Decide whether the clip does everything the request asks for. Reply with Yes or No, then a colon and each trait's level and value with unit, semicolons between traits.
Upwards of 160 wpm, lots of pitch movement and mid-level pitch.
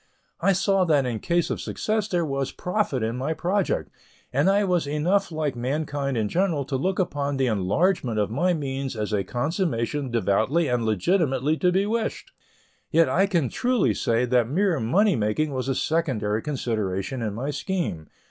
Yes: average, 175 wpm; wide, 7.1 semitones; medium, 145 Hz